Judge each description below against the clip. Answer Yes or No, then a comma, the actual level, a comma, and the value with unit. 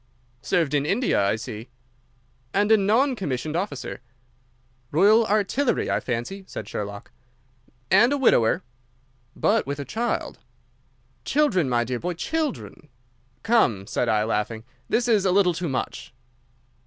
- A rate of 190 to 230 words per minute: No, slow, 135 wpm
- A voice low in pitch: No, medium, 180 Hz